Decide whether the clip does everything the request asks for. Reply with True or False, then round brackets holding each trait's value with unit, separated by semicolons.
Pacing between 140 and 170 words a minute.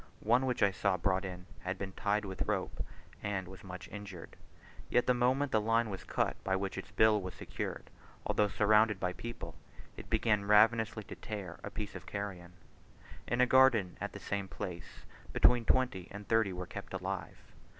False (185 wpm)